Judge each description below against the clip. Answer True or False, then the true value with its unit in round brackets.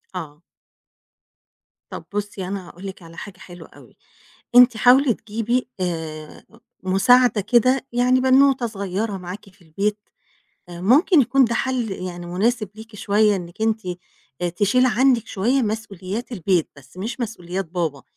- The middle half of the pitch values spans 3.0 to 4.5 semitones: False (5.0 semitones)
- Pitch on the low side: False (205 Hz)